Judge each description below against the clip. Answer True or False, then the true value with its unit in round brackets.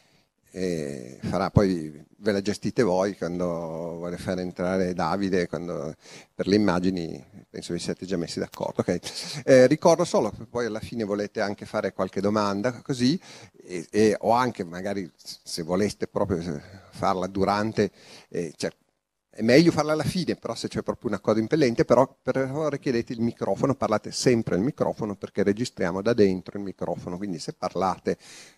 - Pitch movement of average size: True (4.4 semitones)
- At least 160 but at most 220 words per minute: True (165 wpm)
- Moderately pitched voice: False (100 Hz)